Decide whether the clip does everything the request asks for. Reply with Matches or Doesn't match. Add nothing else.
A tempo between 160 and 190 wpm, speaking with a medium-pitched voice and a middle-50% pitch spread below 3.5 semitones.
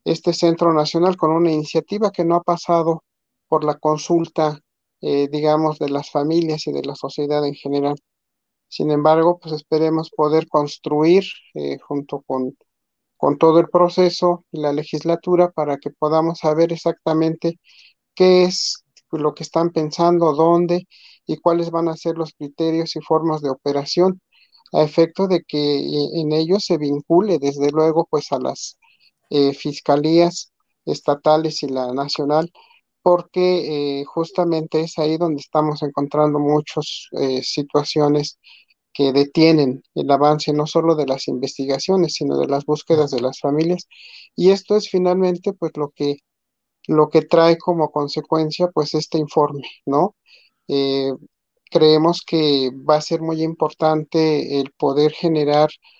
Doesn't match